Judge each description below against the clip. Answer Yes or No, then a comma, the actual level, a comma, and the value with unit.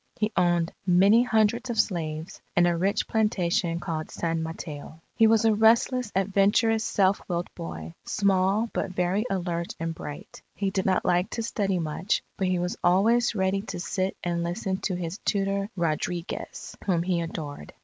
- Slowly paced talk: No, average, 170 wpm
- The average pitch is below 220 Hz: Yes, medium, 185 Hz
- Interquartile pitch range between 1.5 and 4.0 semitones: Yes, average, 3.3 semitones